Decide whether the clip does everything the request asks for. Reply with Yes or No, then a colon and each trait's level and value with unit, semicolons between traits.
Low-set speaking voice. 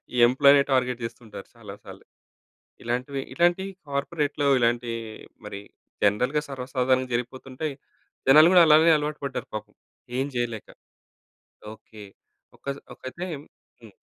Yes: low, 130 Hz